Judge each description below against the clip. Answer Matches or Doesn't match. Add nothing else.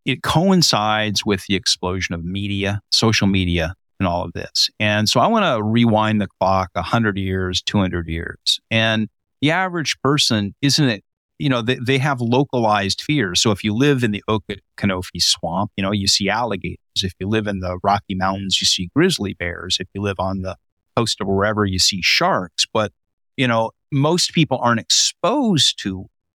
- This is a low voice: Matches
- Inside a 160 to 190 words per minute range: Matches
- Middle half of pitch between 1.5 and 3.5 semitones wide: Doesn't match